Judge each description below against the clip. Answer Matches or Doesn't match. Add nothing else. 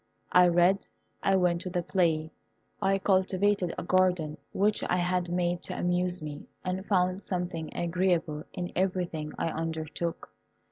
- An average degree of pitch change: Doesn't match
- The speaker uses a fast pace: Doesn't match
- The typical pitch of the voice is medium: Matches